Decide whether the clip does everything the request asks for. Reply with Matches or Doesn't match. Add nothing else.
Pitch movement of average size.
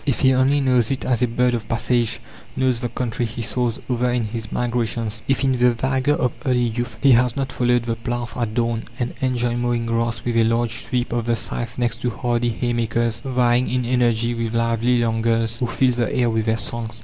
Doesn't match